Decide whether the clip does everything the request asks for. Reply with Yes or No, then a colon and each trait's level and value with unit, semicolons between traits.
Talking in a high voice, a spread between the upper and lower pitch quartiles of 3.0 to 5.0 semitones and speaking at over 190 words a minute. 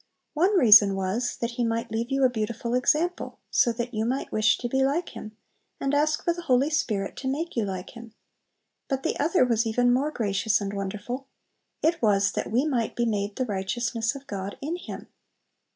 Yes: high, 240 Hz; average, 4.1 semitones; average, 200 wpm